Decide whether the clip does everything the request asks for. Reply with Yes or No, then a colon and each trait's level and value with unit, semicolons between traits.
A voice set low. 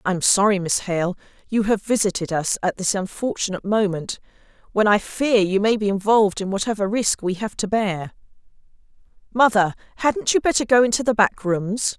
No: high, 205 Hz